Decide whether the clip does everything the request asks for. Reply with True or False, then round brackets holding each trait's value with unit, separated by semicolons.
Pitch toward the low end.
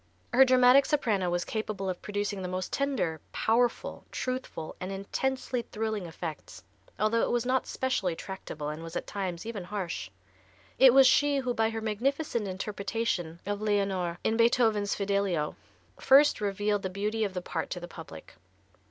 False (205 Hz)